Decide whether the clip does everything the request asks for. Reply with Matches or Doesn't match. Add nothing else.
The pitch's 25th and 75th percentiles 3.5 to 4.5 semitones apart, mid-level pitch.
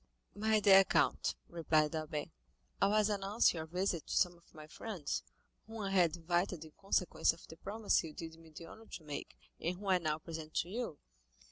Matches